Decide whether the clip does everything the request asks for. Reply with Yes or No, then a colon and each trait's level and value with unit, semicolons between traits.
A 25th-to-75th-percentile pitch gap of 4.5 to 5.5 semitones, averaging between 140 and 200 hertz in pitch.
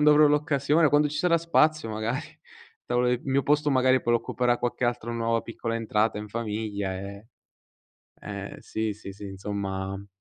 No: average, 5.2 semitones; low, 115 Hz